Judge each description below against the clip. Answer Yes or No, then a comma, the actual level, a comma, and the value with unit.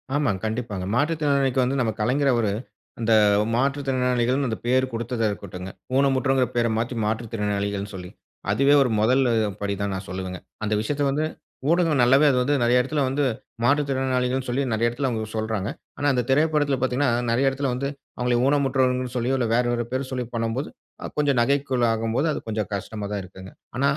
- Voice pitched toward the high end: No, low, 125 Hz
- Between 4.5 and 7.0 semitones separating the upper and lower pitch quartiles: No, average, 3.4 semitones